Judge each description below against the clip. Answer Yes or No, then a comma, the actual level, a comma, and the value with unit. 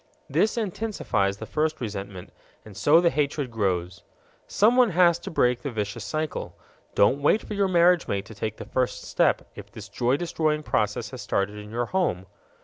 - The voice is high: No, low, 130 Hz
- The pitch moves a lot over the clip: Yes, wide, 8.6 semitones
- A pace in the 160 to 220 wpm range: Yes, average, 180 wpm